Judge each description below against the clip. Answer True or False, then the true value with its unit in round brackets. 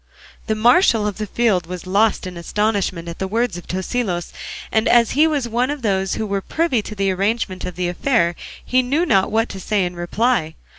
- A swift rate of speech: True (210 wpm)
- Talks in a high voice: True (210 Hz)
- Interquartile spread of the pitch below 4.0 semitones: False (4.6 semitones)